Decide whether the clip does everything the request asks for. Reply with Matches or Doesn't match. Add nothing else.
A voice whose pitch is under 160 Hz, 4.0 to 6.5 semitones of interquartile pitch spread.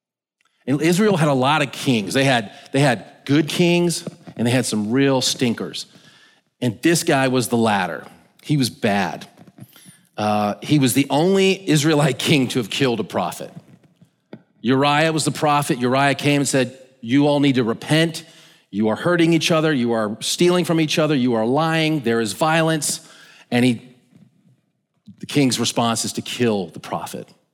Matches